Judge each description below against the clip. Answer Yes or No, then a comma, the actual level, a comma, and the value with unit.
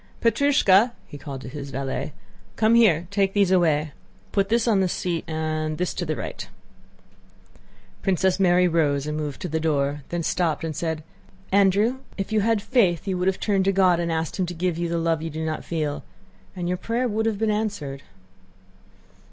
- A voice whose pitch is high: No, medium, 175 Hz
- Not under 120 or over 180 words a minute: No, average, 195 wpm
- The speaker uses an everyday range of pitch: Yes, average, 4.1 semitones